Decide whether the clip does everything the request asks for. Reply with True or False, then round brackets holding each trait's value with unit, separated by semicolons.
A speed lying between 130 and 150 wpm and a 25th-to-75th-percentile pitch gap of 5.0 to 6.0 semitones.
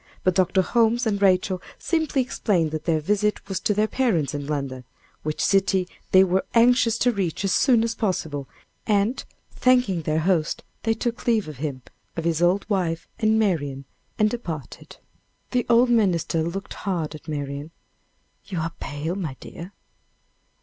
False (165 wpm; 5.6 semitones)